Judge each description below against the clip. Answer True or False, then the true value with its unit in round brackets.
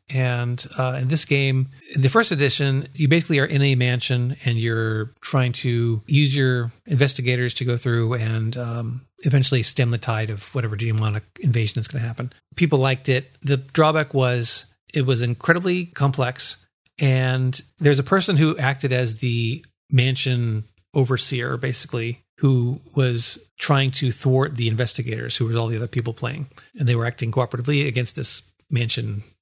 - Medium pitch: False (125 Hz)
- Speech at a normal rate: True (165 wpm)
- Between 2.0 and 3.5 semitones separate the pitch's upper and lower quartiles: True (2.8 semitones)